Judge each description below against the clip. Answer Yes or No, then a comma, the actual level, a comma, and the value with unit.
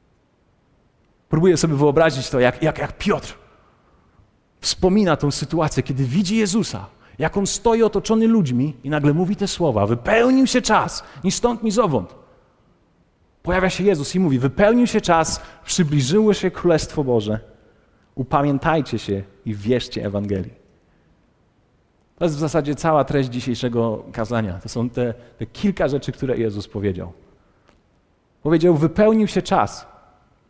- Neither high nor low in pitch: Yes, medium, 150 Hz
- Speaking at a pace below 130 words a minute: No, average, 135 wpm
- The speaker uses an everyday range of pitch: No, wide, 7.6 semitones